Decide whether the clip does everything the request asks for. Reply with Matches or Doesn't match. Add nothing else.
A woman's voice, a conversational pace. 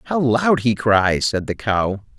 Doesn't match